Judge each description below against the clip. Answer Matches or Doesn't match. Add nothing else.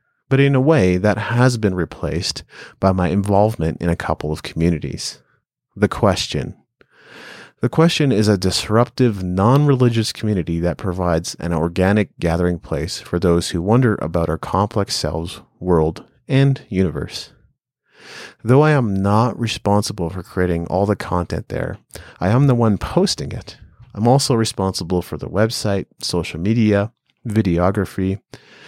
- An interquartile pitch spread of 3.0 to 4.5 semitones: Doesn't match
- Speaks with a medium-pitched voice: Doesn't match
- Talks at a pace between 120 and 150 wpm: Matches